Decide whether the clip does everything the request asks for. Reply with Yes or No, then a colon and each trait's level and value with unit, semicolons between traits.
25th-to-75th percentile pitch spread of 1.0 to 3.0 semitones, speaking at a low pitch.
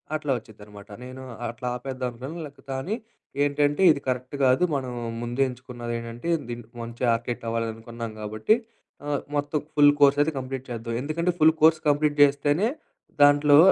No: average, 3.6 semitones; low, 130 Hz